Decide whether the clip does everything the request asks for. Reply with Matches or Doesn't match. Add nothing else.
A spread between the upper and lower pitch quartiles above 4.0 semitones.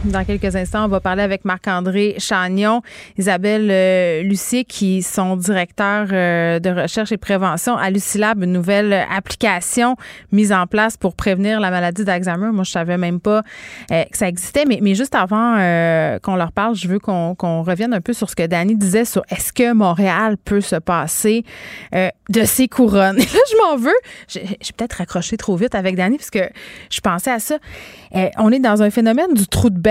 Doesn't match